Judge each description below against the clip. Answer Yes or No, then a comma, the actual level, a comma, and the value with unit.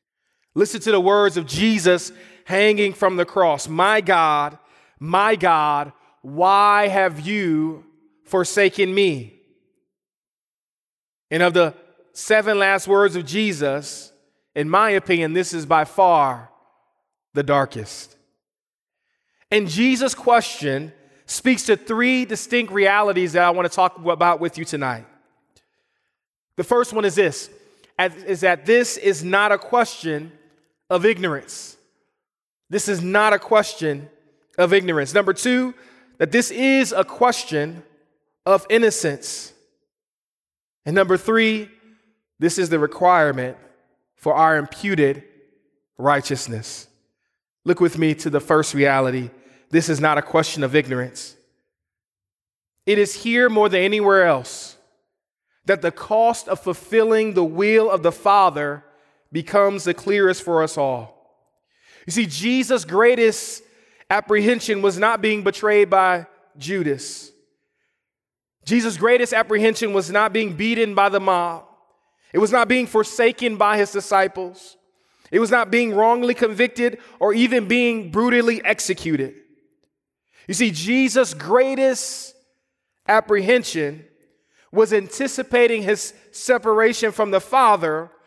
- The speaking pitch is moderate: No, high, 195 Hz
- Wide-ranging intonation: Yes, wide, 5.9 semitones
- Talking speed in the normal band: No, slow, 125 wpm